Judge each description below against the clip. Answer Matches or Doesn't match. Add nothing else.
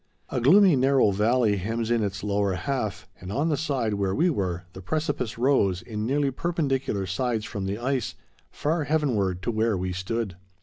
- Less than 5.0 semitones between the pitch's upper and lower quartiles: Doesn't match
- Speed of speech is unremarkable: Matches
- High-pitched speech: Doesn't match